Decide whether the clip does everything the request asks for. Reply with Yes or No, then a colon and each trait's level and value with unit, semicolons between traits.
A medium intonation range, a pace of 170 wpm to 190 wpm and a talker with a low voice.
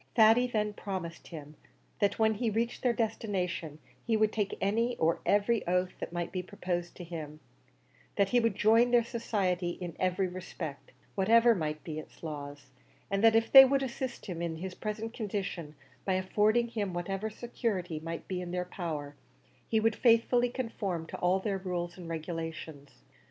No: average, 4.6 semitones; average, 175 wpm; high, 190 Hz